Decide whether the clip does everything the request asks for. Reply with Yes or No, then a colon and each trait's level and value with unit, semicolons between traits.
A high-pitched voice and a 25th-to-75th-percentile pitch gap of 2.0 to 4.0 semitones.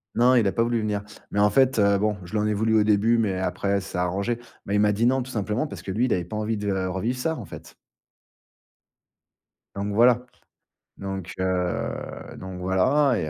No: low, 105 Hz; average, 3.4 semitones